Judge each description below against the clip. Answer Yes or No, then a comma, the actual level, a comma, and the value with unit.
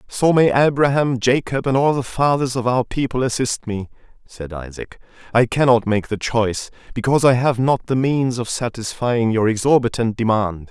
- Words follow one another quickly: No, average, 175 wpm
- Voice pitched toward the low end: Yes, low, 120 Hz